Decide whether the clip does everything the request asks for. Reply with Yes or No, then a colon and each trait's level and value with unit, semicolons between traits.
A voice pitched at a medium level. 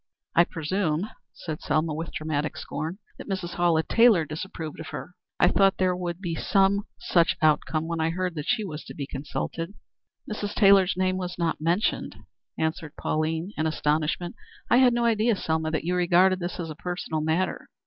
Yes: medium, 170 Hz